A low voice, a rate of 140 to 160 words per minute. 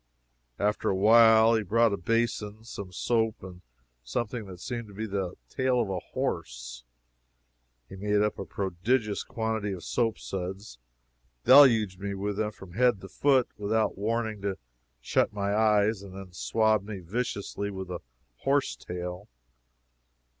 Yes: low, 105 Hz; average, 155 wpm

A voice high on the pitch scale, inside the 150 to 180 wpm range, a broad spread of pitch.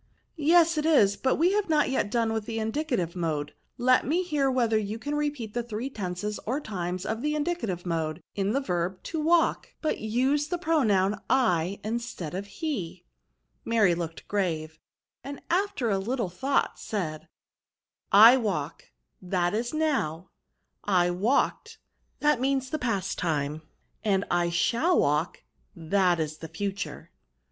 Yes: high, 215 Hz; average, 165 wpm; wide, 7.6 semitones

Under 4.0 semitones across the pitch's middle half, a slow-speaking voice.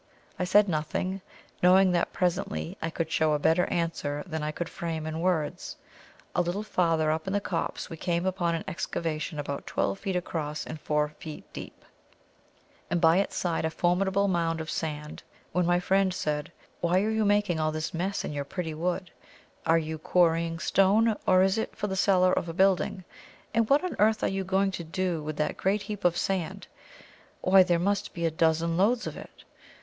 No: average, 3.1 semitones; average, 195 wpm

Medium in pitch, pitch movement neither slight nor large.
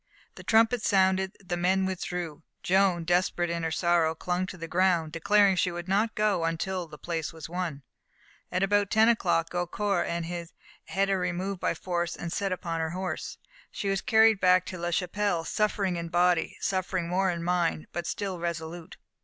No: medium, 180 Hz; narrow, 2.2 semitones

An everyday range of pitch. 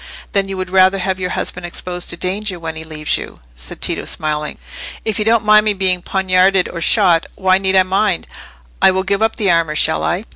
No: narrow, 2.1 semitones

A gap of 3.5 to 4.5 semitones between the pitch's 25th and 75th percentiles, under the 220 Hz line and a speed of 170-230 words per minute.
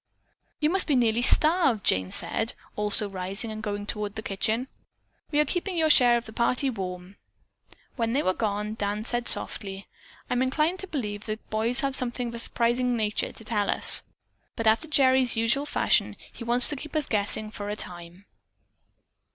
No: average, 3.9 semitones; high, 230 Hz; average, 185 wpm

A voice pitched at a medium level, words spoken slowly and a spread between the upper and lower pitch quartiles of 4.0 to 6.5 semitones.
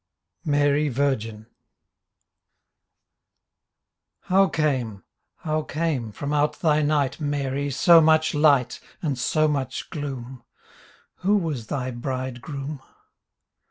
No: medium, 145 Hz; slow, 95 wpm; average, 3.0 semitones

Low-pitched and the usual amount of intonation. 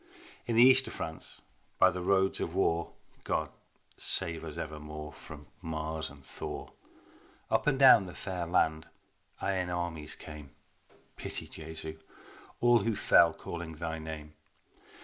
Yes: very low, 80 Hz; average, 3.3 semitones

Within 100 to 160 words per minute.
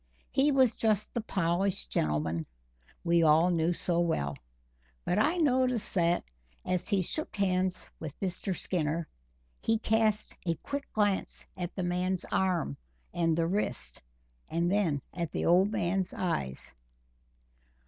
Yes: average, 140 wpm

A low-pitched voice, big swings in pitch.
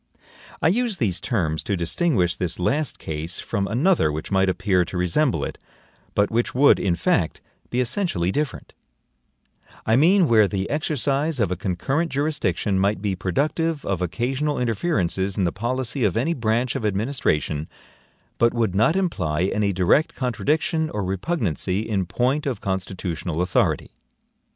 Yes: low, 110 Hz; wide, 7.4 semitones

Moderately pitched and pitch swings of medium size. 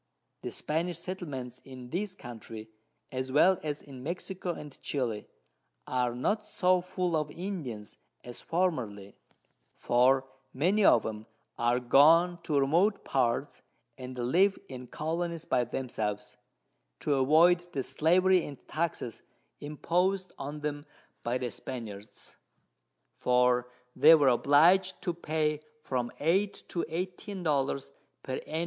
No: medium, 145 Hz; wide, 5.8 semitones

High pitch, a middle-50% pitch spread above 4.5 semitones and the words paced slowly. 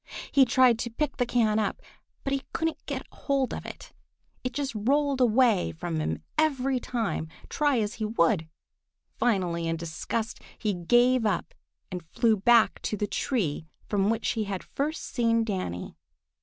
No: high, 225 Hz; average, 5.0 semitones; average, 165 wpm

